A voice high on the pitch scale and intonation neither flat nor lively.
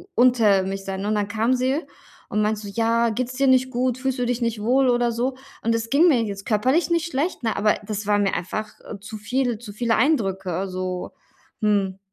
Yes: high, 225 Hz; average, 3.7 semitones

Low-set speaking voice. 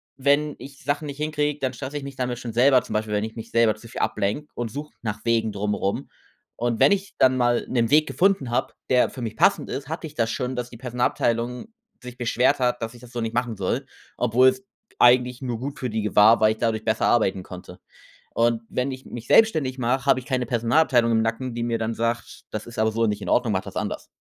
Yes: low, 120 Hz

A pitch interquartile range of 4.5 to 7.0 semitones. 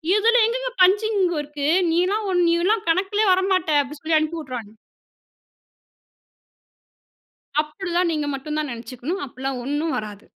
Yes: average, 5.1 semitones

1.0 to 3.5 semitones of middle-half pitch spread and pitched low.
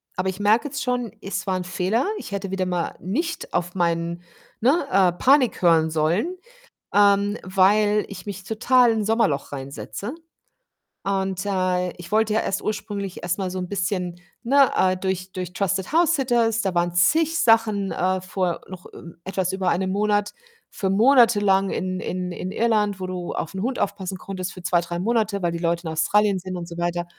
No: average, 2.9 semitones; high, 190 Hz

